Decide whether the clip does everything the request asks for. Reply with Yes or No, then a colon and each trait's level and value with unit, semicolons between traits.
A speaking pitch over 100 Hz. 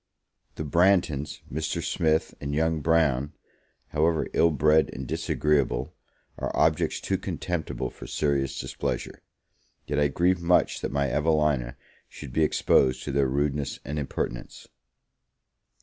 No: very low, 75 Hz